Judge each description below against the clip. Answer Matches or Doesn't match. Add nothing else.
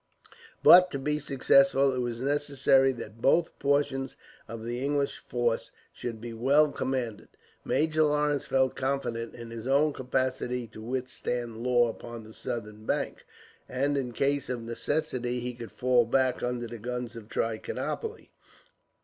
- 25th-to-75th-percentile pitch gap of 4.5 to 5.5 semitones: Doesn't match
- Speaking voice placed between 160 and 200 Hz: Doesn't match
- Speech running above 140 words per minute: Matches